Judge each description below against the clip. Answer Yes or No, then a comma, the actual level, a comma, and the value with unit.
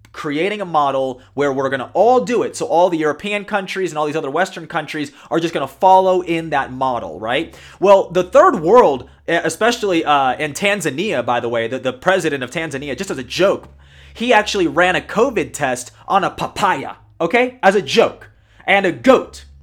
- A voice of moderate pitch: Yes, medium, 165 Hz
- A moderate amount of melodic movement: No, wide, 6.0 semitones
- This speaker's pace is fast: No, average, 195 wpm